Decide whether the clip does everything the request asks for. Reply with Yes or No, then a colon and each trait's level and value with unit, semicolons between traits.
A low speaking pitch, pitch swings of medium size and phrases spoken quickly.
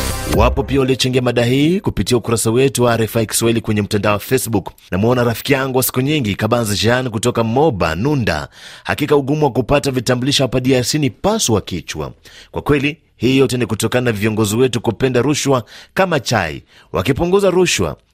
Yes: low, 125 Hz; average, 3.6 semitones; fast, 165 wpm